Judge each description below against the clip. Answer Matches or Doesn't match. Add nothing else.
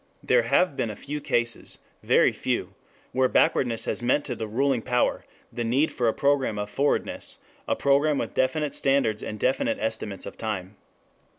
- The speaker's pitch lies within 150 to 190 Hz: Doesn't match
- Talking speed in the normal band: Matches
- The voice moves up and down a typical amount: Matches